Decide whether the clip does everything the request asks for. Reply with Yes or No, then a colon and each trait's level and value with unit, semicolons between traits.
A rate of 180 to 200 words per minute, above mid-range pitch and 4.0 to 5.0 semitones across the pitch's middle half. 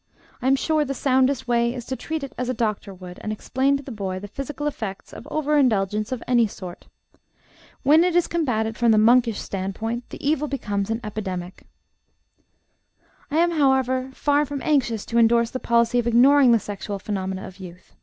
Yes: average, 195 wpm; high, 240 Hz; average, 4.6 semitones